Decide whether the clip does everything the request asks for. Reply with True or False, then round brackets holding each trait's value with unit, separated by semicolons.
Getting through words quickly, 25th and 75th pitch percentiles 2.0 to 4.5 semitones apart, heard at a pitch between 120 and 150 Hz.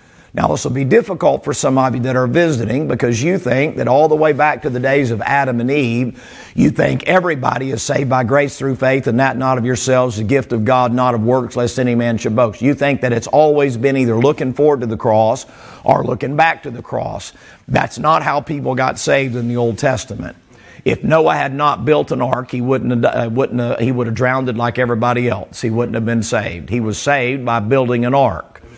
True (235 wpm; 2.5 semitones; 125 Hz)